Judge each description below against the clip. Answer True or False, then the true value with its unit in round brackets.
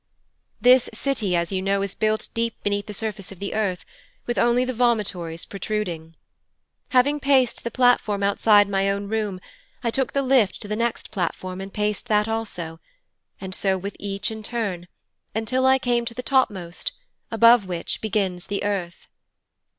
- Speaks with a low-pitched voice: False (210 Hz)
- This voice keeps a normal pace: True (170 wpm)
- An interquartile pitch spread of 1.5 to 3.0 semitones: False (3.5 semitones)